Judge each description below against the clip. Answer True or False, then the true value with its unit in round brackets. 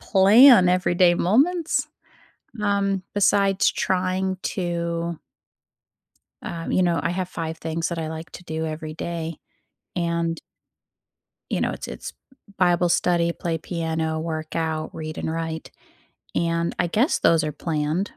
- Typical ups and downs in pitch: False (2.2 semitones)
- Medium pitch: True (170 Hz)